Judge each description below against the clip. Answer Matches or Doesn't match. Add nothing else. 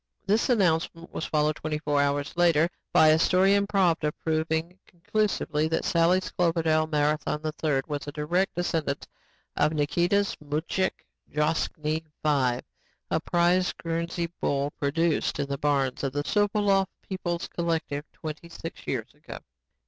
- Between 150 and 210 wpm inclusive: Doesn't match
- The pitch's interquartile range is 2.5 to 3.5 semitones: Matches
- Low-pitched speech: Doesn't match